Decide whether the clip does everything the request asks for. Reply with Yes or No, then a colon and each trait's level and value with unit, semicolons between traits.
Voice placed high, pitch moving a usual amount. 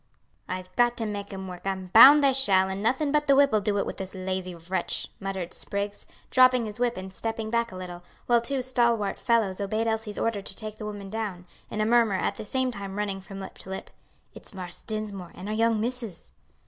Yes: high, 210 Hz; average, 3.5 semitones